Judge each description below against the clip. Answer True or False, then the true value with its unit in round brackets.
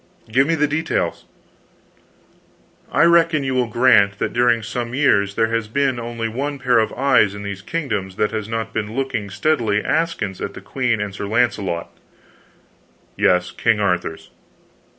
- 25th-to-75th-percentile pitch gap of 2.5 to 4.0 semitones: False (4.6 semitones)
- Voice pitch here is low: True (115 Hz)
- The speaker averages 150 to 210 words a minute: True (165 wpm)